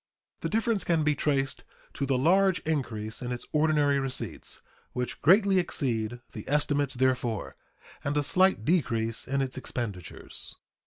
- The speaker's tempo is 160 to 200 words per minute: No, average, 145 wpm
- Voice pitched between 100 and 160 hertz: Yes, medium, 140 Hz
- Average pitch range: Yes, average, 4.4 semitones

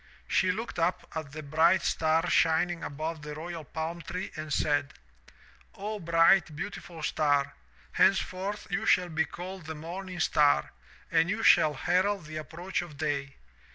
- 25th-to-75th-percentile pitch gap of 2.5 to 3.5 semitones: Yes, average, 3.0 semitones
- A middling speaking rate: Yes, average, 155 wpm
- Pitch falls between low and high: Yes, medium, 165 Hz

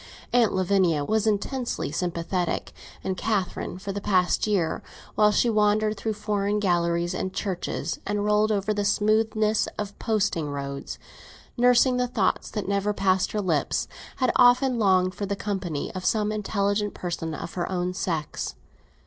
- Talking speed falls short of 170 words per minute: Yes, average, 155 wpm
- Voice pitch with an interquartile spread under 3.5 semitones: Yes, average, 2.8 semitones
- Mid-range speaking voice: No, high, 200 Hz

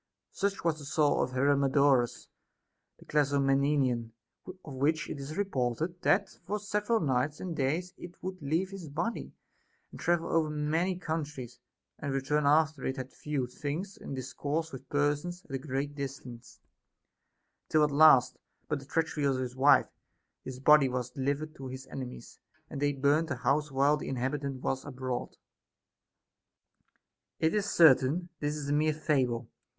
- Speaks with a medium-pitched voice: Yes, medium, 145 Hz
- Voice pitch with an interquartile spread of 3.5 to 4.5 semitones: No, average, 3.0 semitones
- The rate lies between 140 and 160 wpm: Yes, average, 155 wpm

